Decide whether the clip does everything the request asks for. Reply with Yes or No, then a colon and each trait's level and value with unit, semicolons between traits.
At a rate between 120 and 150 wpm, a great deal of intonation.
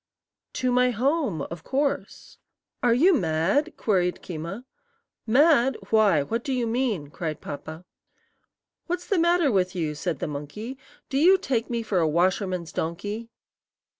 Yes: average, 145 wpm; wide, 7.8 semitones